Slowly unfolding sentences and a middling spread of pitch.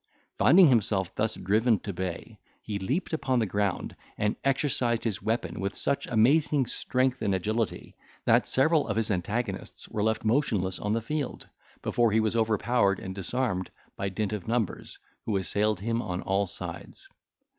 No: average, 165 wpm; average, 3.8 semitones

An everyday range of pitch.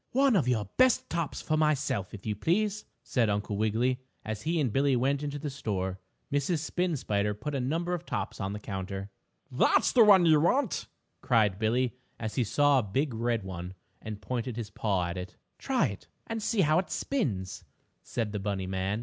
No: wide, 7.1 semitones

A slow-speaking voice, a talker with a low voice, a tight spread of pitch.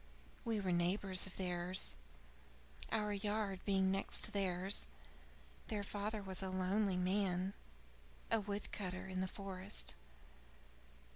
No: slow, 125 wpm; high, 195 Hz; narrow, 1.7 semitones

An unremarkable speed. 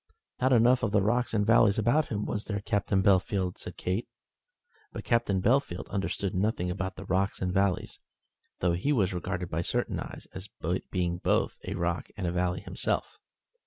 Yes: average, 180 wpm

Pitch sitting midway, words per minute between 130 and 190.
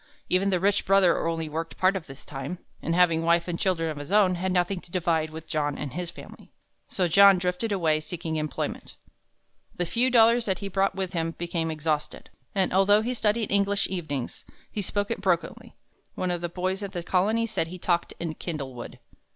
No: medium, 180 Hz; average, 200 wpm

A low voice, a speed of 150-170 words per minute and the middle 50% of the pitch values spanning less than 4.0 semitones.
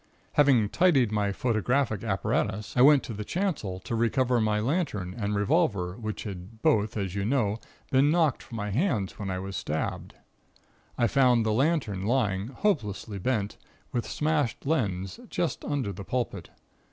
No: low, 110 Hz; average, 160 wpm; average, 4.9 semitones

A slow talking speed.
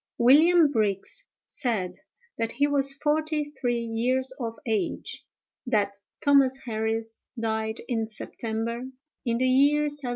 Yes: slow, 125 wpm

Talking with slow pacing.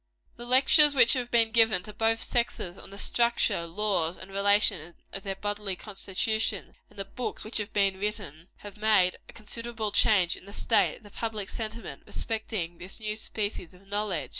No: average, 180 wpm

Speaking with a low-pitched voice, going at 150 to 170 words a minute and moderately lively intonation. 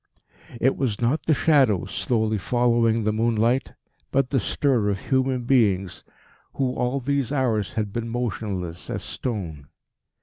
No: low, 115 Hz; average, 140 wpm; average, 3.6 semitones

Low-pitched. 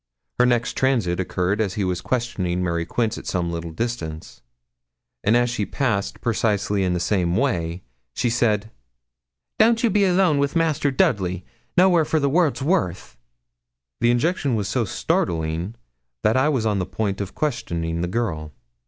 Yes: low, 110 Hz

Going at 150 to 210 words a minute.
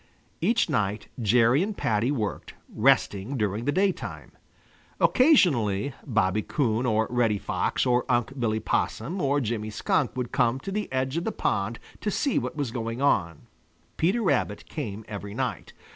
Yes: average, 160 wpm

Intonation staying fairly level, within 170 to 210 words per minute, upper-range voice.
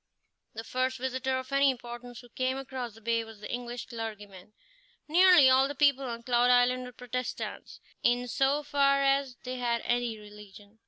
Yes: narrow, 2.2 semitones; average, 175 wpm; very high, 250 Hz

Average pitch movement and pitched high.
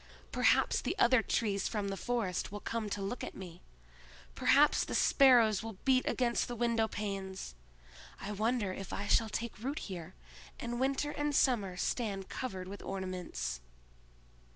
Yes: average, 3.9 semitones; high, 215 Hz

